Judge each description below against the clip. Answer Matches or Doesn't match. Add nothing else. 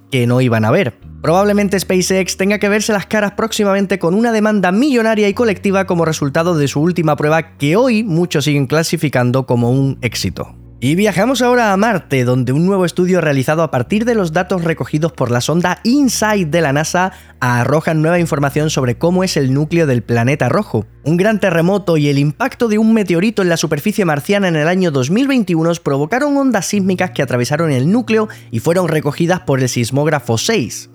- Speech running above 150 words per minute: Matches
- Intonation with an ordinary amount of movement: Doesn't match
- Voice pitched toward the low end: Doesn't match